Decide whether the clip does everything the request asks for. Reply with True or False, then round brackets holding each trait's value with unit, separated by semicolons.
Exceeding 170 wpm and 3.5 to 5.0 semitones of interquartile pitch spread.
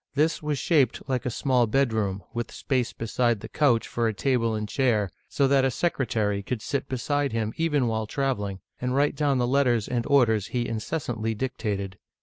True (185 wpm; 3.8 semitones)